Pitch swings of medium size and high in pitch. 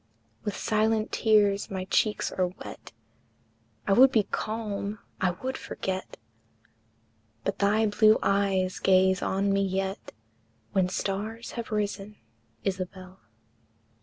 No: narrow, 2.2 semitones; high, 200 Hz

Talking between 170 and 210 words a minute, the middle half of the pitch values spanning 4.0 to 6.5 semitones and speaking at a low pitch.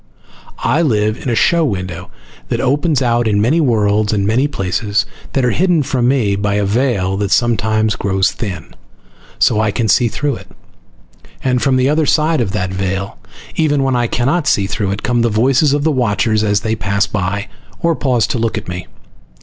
Yes: average, 200 wpm; average, 4.8 semitones; low, 115 Hz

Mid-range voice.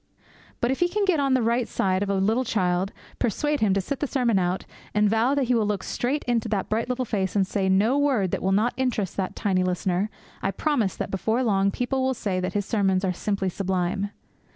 No: high, 210 Hz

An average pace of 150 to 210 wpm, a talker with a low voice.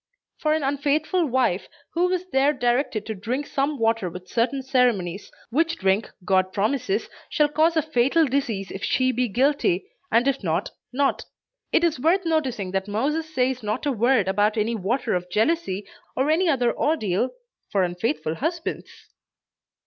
No: average, 165 wpm; very high, 250 Hz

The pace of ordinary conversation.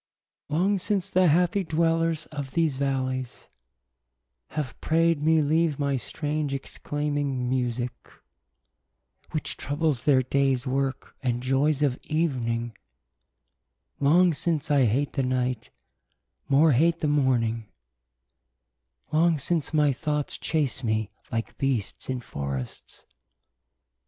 No: slow, 115 wpm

